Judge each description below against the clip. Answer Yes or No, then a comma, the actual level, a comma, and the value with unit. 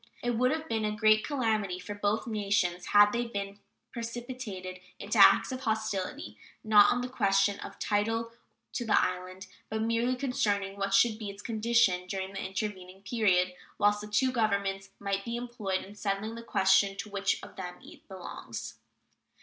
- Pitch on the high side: Yes, high, 205 Hz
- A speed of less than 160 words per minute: No, average, 175 wpm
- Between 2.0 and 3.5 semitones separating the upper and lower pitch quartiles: Yes, average, 2.8 semitones